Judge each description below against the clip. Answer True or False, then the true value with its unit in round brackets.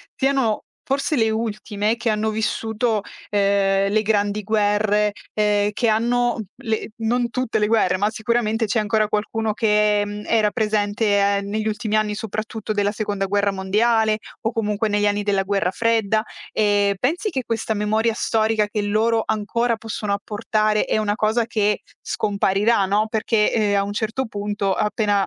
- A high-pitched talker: True (215 Hz)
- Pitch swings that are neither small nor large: False (1.4 semitones)